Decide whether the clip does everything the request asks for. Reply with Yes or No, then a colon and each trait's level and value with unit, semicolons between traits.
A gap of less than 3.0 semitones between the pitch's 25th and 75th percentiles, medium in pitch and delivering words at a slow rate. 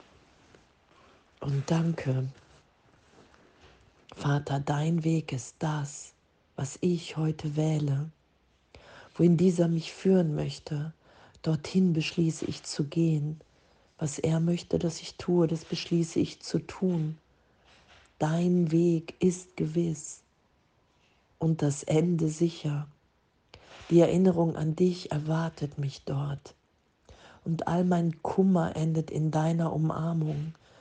Yes: narrow, 2.5 semitones; medium, 160 Hz; slow, 105 wpm